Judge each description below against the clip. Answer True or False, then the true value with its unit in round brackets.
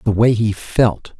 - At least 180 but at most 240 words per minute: True (200 wpm)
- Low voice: True (110 Hz)